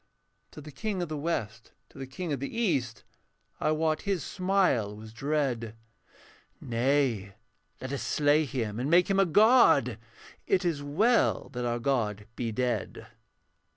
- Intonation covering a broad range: Yes, wide, 6.2 semitones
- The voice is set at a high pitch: No, medium, 140 Hz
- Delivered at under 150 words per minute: No, average, 155 wpm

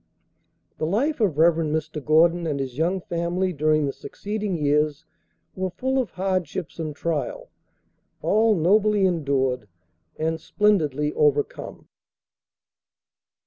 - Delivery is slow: Yes, slow, 115 wpm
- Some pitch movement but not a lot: Yes, average, 4.2 semitones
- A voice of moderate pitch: Yes, medium, 165 Hz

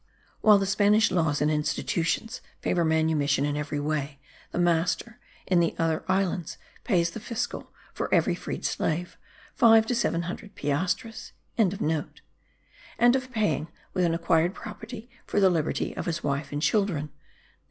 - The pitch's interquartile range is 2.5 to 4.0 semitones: No, average, 5.3 semitones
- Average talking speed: Yes, average, 150 wpm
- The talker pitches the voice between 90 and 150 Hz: No, medium, 175 Hz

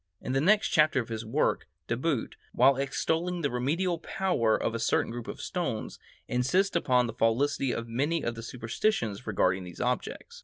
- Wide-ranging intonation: Yes, wide, 6.0 semitones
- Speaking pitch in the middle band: No, low, 130 Hz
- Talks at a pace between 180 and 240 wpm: Yes, average, 185 wpm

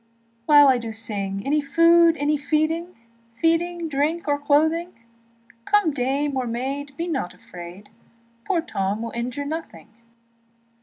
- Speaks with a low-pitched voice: No, very high, 290 Hz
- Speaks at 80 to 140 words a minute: Yes, slow, 135 wpm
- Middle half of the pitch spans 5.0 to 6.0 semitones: Yes, wide, 5.4 semitones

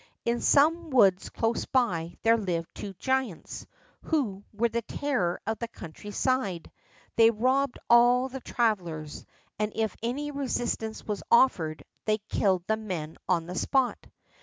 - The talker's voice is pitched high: Yes, high, 220 Hz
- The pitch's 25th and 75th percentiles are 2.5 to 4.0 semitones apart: No, average, 5.2 semitones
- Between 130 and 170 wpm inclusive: Yes, average, 145 wpm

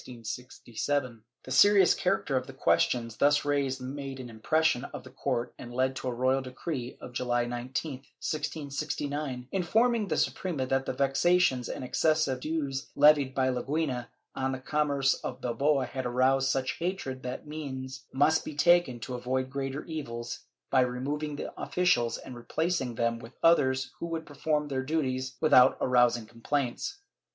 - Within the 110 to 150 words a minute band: No, average, 160 wpm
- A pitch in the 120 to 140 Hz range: Yes, low, 135 Hz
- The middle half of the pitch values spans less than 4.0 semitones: Yes, average, 3.0 semitones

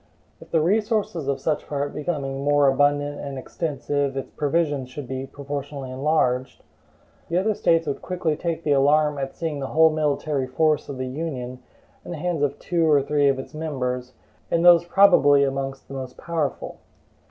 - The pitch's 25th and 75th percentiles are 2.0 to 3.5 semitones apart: Yes, average, 3.0 semitones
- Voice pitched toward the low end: No, medium, 145 Hz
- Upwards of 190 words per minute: No, average, 175 wpm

